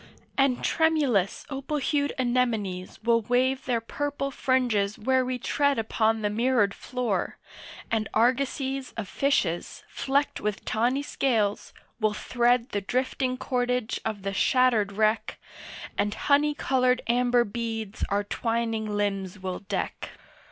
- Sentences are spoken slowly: Yes, slow, 130 wpm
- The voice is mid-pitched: No, high, 240 Hz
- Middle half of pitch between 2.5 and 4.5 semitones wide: Yes, average, 3.7 semitones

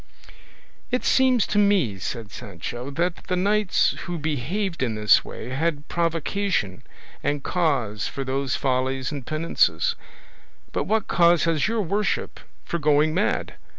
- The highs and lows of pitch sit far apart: Yes, wide, 5.9 semitones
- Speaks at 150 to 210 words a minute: No, average, 140 wpm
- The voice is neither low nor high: Yes, medium, 155 Hz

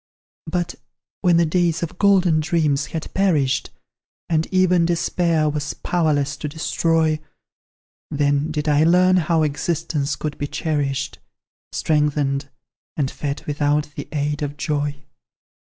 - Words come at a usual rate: No, slow, 125 wpm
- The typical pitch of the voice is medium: Yes, medium, 155 Hz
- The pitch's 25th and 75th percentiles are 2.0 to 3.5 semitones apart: Yes, narrow, 2.6 semitones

